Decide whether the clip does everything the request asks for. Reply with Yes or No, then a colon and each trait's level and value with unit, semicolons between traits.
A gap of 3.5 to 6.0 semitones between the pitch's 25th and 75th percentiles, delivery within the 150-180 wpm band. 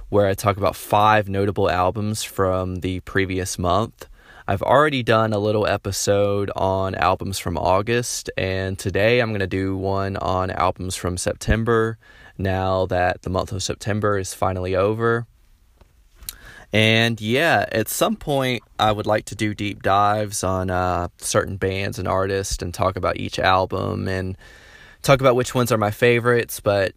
No: narrow, 2.4 semitones; average, 160 wpm